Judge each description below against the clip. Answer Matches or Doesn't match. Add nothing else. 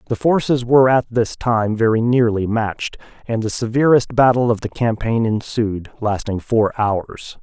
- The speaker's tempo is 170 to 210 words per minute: Doesn't match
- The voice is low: Matches